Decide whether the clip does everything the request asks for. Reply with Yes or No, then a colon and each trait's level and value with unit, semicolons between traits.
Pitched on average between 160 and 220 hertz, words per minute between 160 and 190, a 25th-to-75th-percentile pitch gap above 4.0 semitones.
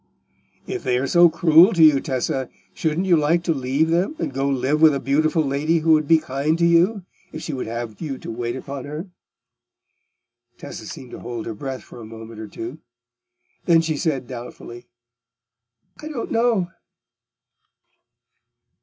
No: medium, 150 Hz; average, 175 wpm; average, 4.5 semitones